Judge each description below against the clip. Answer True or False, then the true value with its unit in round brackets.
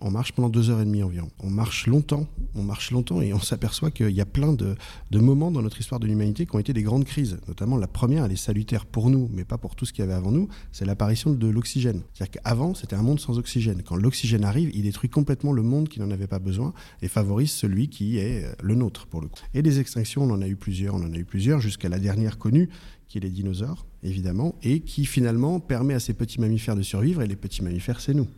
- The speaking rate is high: True (265 wpm)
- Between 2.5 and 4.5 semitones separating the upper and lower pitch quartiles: False (5.1 semitones)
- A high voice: False (115 Hz)